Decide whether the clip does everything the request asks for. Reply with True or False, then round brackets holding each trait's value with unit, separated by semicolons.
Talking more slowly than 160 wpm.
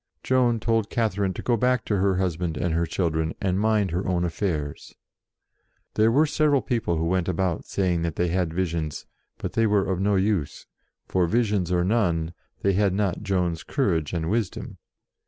False (180 wpm)